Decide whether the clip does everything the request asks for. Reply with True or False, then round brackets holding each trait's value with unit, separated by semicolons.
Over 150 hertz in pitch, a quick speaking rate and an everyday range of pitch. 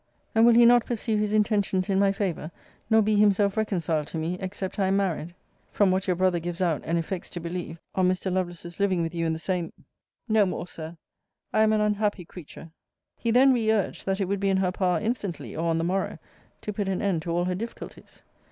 True (190 Hz; 230 wpm; 3.3 semitones)